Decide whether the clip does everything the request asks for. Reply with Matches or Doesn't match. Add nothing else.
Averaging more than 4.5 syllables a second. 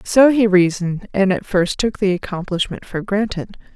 Matches